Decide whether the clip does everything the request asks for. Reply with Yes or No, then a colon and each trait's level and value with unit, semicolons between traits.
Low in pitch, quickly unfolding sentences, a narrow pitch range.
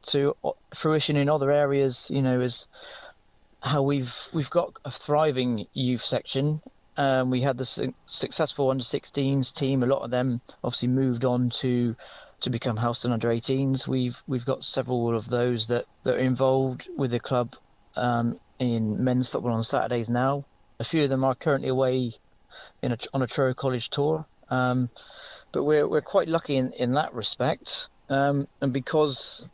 No: low, 130 Hz; average, 175 wpm; narrow, 2.3 semitones